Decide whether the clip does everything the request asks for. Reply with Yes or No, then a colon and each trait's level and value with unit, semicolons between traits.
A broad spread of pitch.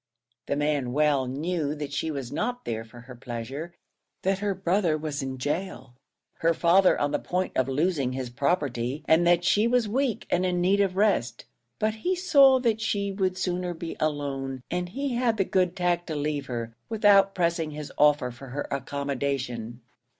Yes: wide, 5.8 semitones